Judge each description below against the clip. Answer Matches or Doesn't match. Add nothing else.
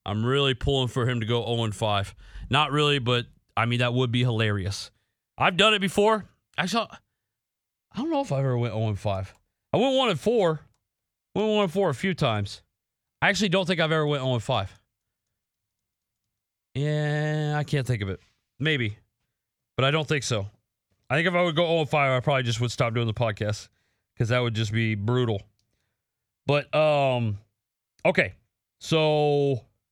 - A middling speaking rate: Matches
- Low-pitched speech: Matches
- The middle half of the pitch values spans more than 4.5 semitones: Matches